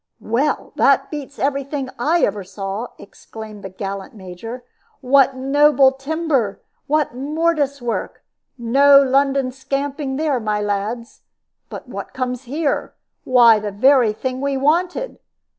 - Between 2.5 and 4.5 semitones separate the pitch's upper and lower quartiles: Yes, average, 3.9 semitones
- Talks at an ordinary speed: No, slow, 130 wpm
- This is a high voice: Yes, very high, 265 Hz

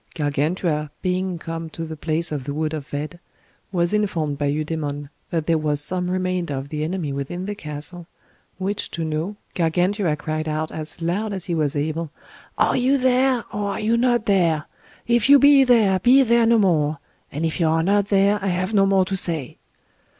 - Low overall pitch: No, medium, 170 Hz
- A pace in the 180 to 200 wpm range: Yes, average, 195 wpm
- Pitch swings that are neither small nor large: Yes, average, 4.6 semitones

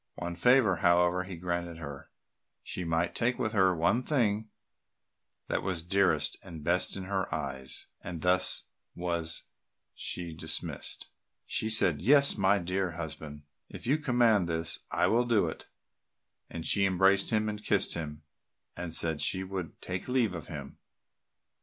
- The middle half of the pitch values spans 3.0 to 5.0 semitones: Yes, average, 3.7 semitones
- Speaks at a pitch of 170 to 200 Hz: No, very low, 90 Hz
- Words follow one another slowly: No, average, 155 wpm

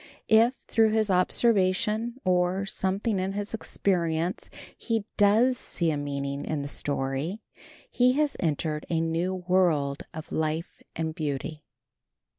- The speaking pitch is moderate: Yes, medium, 180 Hz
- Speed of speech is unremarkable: No, slow, 130 wpm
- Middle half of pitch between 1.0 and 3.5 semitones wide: No, average, 5.2 semitones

